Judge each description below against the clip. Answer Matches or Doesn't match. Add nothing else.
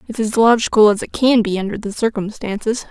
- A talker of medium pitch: Doesn't match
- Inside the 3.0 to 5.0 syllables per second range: Doesn't match